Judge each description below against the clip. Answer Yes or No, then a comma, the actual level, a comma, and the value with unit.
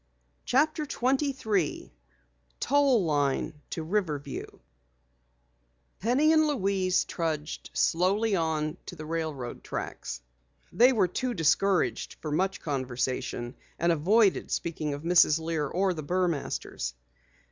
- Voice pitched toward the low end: No, medium, 170 Hz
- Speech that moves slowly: Yes, slow, 110 wpm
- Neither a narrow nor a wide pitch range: No, wide, 6.0 semitones